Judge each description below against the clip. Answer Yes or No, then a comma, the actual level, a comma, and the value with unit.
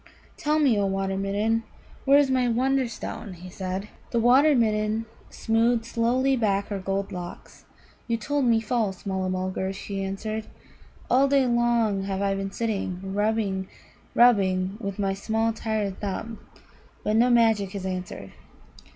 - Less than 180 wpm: Yes, average, 150 wpm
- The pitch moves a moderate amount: Yes, average, 3.4 semitones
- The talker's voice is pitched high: Yes, high, 215 Hz